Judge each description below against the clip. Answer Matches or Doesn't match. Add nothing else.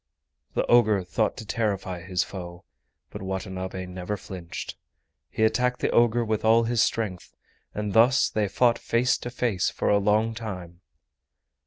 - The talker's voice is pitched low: Matches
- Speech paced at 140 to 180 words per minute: Matches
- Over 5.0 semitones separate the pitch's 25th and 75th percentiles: Doesn't match